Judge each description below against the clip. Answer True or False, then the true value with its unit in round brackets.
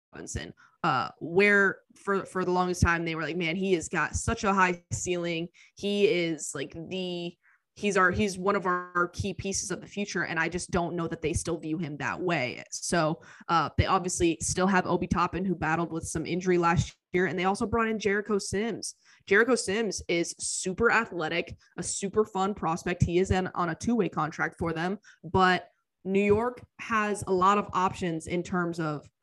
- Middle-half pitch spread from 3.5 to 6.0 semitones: False (2.8 semitones)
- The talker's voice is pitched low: False (180 Hz)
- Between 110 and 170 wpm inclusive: False (200 wpm)